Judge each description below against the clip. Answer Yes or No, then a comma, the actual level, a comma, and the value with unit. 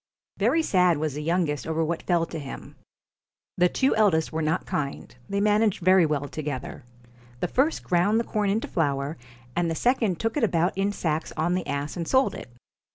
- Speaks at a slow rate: No, average, 195 wpm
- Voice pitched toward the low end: No, medium, 175 Hz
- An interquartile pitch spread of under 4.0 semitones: No, average, 4.7 semitones